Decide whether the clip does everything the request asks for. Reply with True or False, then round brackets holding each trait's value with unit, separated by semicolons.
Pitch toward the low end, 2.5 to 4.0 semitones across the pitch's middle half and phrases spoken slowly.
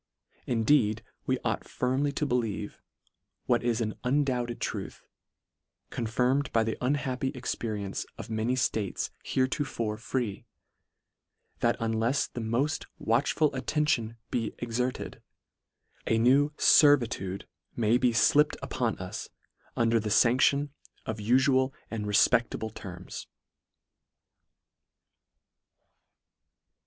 True (120 Hz; 2.9 semitones; 105 wpm)